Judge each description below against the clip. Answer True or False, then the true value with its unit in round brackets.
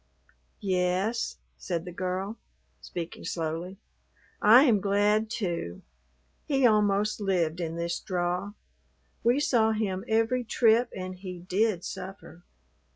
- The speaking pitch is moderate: False (195 Hz)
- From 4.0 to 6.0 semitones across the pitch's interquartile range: False (3.5 semitones)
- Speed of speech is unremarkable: False (115 wpm)